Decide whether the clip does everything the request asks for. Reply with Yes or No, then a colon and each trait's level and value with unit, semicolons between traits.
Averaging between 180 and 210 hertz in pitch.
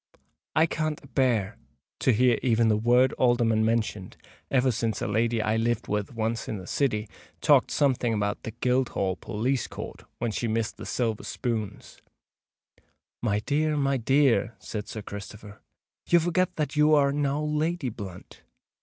No: low, 120 Hz